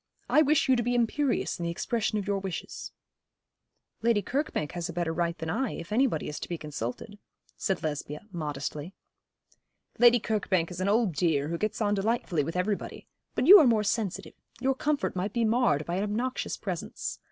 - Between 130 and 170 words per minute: No, average, 190 wpm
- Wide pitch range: Yes, wide, 5.9 semitones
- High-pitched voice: Yes, high, 200 Hz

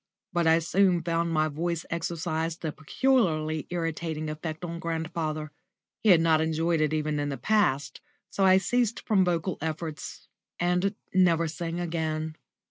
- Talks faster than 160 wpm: No, average, 150 wpm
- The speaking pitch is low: No, medium, 165 Hz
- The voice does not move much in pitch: Yes, narrow, 1.9 semitones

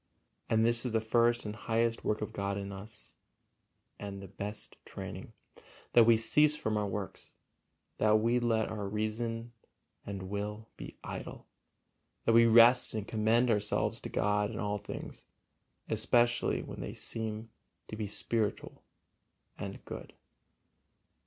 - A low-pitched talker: Yes, low, 110 Hz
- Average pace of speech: Yes, average, 145 wpm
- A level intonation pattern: Yes, narrow, 1.9 semitones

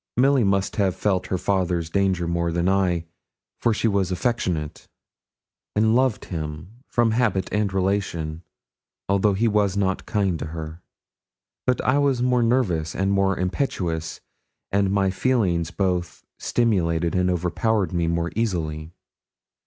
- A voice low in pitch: Yes, very low, 95 Hz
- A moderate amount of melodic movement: Yes, average, 3.8 semitones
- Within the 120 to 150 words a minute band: Yes, average, 140 wpm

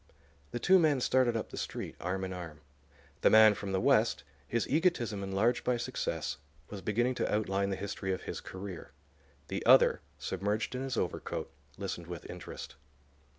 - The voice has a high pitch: No, low, 105 Hz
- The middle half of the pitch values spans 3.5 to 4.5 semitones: Yes, average, 4.1 semitones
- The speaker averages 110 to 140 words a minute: No, average, 170 wpm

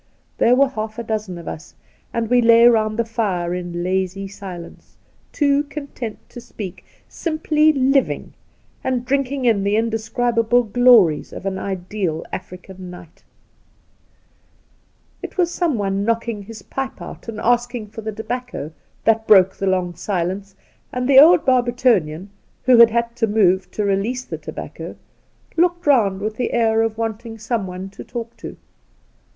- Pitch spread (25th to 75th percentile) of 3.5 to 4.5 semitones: Yes, average, 4.0 semitones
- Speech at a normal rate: Yes, average, 155 wpm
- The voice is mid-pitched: No, high, 225 Hz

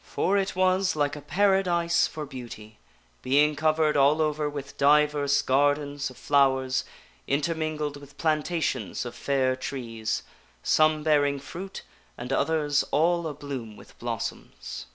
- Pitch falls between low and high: Yes, medium, 145 Hz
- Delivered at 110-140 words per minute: Yes, slow, 135 wpm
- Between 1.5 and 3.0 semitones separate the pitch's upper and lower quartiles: Yes, narrow, 2.4 semitones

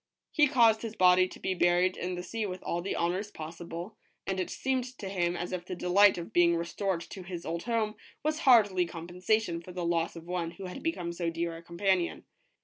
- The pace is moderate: No, fast, 220 wpm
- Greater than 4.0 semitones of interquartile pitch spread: No, average, 3.0 semitones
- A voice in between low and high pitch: Yes, medium, 180 Hz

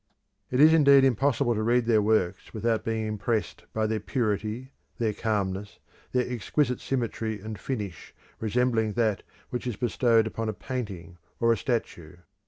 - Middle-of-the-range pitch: No, low, 110 Hz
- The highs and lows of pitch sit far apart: No, average, 2.7 semitones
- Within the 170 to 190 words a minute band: No, average, 155 wpm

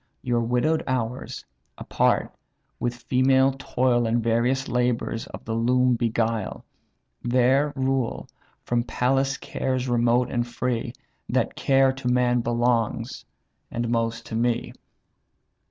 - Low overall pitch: Yes, low, 120 Hz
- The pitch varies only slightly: Yes, narrow, 1.7 semitones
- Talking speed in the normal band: No, slow, 120 wpm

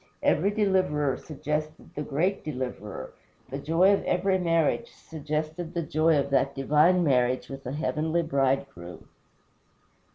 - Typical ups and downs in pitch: Yes, average, 3.7 semitones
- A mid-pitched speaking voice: Yes, medium, 155 Hz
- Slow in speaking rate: Yes, slow, 130 wpm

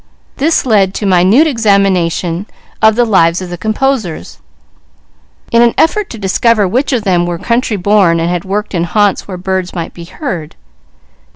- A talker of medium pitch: No, high, 195 Hz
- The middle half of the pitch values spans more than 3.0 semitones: Yes, average, 4.6 semitones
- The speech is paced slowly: No, average, 170 wpm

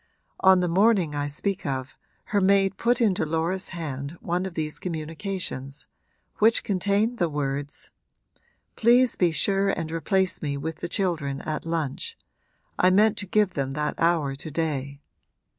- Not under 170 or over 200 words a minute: No, average, 155 wpm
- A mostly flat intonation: No, average, 4.7 semitones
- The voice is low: No, medium, 170 Hz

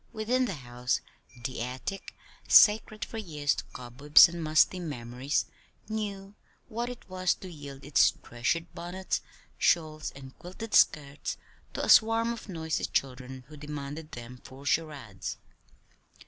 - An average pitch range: No, wide, 6.4 semitones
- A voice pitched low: No, medium, 155 Hz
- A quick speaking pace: No, slow, 135 wpm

